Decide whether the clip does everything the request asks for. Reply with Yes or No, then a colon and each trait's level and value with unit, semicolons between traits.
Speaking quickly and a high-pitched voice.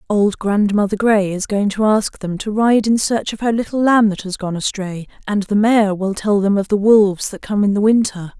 Yes: fast, 245 wpm; high, 205 Hz